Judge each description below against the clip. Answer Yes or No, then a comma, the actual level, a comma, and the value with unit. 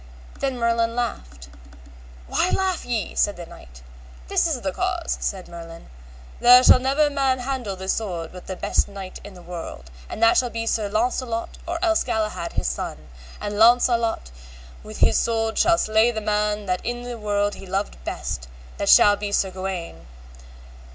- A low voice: No, high, 210 Hz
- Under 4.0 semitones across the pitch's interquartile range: No, average, 4.8 semitones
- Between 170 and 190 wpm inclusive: Yes, average, 175 wpm